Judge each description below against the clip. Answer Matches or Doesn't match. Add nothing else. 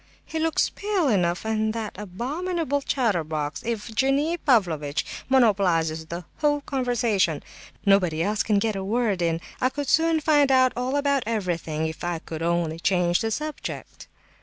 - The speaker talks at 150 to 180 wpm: Matches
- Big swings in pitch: Matches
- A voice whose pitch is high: Matches